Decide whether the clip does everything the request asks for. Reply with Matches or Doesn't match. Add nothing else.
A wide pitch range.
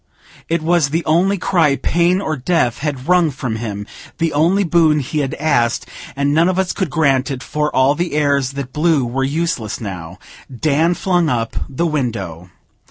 Doesn't match